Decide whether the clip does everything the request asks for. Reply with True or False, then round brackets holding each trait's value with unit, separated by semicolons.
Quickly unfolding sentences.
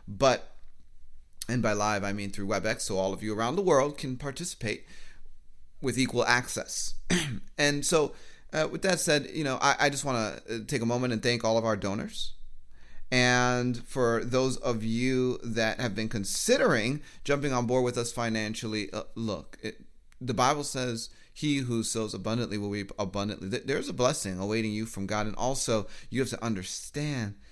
False (180 wpm)